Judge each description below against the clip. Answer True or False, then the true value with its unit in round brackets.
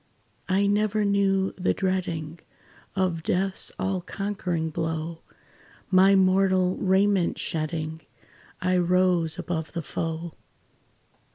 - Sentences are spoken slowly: True (100 wpm)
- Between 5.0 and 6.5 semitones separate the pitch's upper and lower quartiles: False (2.7 semitones)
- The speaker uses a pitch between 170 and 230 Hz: True (185 Hz)